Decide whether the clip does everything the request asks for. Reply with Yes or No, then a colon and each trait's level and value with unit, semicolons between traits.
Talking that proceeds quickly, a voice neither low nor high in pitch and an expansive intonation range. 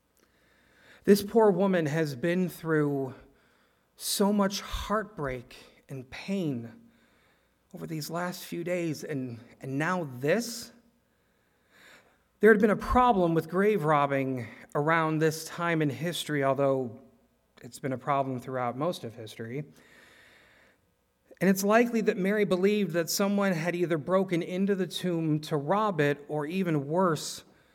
No: slow, 135 wpm; medium, 160 Hz; wide, 6.0 semitones